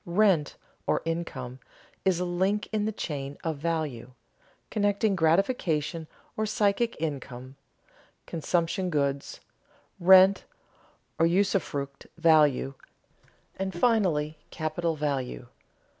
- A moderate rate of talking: No, slow, 100 wpm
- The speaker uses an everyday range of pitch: Yes, average, 4.6 semitones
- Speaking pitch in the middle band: Yes, medium, 165 Hz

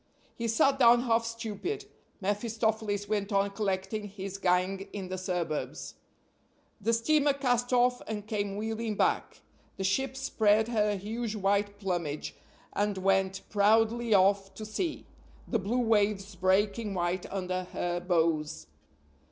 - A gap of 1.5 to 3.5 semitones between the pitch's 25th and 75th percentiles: Yes, average, 2.9 semitones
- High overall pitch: Yes, high, 205 Hz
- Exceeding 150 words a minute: No, slow, 135 wpm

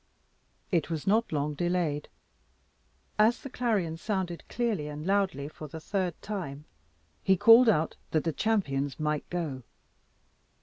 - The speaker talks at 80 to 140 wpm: Yes, slow, 135 wpm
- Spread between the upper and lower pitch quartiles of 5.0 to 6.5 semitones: Yes, average, 5.3 semitones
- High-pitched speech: No, medium, 170 Hz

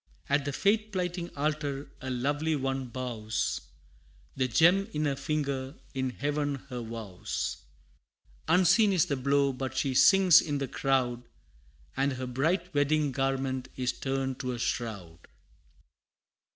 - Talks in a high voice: No, low, 135 Hz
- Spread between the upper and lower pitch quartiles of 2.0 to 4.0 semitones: Yes, average, 2.9 semitones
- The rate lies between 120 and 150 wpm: Yes, average, 140 wpm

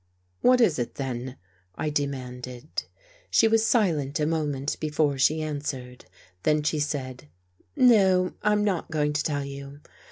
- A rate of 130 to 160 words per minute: Yes, average, 155 wpm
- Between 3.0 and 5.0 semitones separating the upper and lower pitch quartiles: Yes, average, 3.5 semitones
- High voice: No, medium, 145 Hz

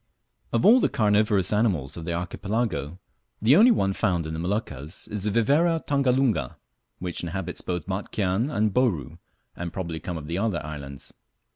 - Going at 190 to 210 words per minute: No, average, 165 wpm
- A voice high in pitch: No, very low, 95 Hz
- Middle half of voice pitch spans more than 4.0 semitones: Yes, average, 5.3 semitones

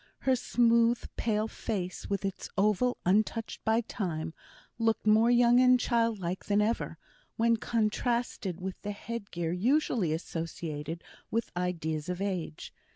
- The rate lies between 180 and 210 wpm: No, slow, 135 wpm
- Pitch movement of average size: Yes, average, 4.5 semitones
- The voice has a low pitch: No, high, 210 Hz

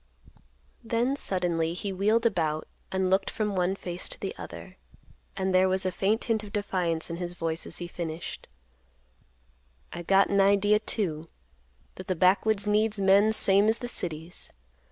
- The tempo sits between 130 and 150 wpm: No, average, 165 wpm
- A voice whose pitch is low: No, high, 190 Hz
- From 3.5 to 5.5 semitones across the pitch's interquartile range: No, average, 3.1 semitones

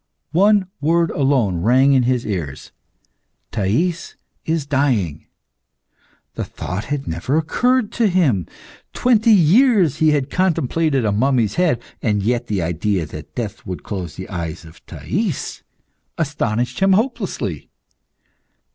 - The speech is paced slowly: Yes, slow, 130 wpm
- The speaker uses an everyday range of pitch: No, wide, 9.0 semitones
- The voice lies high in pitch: No, low, 130 Hz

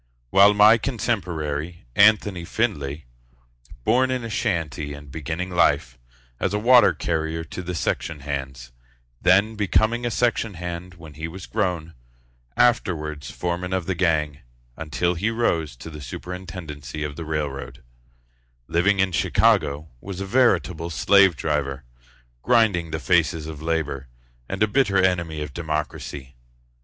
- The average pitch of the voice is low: Yes, very low, 85 Hz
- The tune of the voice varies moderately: Yes, average, 4.7 semitones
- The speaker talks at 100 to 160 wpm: Yes, average, 140 wpm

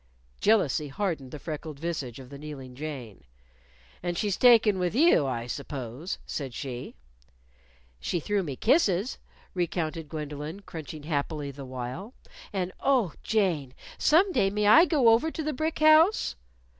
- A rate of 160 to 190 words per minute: No, average, 145 wpm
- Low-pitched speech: No, medium, 165 Hz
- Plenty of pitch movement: Yes, wide, 7.2 semitones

